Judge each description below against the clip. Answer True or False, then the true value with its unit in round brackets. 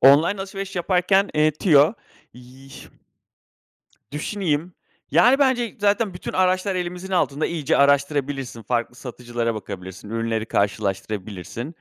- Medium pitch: True (145 Hz)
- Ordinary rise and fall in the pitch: False (7.8 semitones)